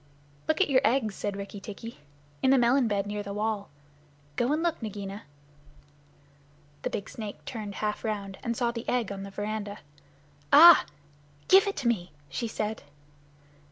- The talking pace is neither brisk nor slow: Yes, average, 170 wpm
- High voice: Yes, high, 215 Hz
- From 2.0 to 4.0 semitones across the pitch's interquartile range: Yes, average, 3.5 semitones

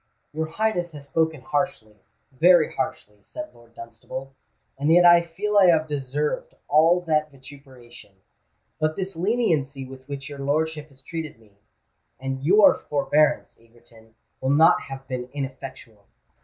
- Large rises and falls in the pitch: No, average, 3.8 semitones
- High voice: No, medium, 145 Hz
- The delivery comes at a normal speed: No, slow, 130 wpm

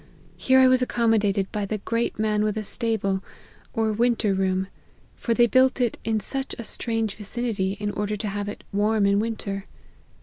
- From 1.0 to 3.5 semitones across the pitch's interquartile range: Yes, narrow, 2.5 semitones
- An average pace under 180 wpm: No, average, 190 wpm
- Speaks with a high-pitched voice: Yes, high, 215 Hz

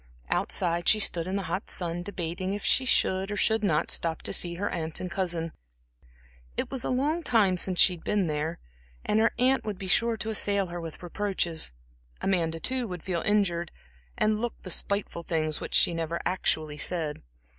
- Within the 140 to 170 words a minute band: No, average, 195 wpm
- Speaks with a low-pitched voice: No, medium, 185 Hz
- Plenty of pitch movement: No, average, 3.7 semitones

